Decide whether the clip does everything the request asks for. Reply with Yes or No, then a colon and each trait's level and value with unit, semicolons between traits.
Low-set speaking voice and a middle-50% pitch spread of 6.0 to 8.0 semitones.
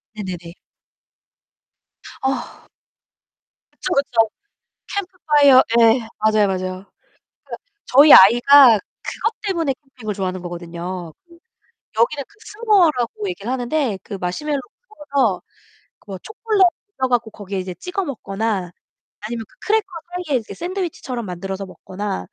No: high, 230 Hz; wide, 7.4 semitones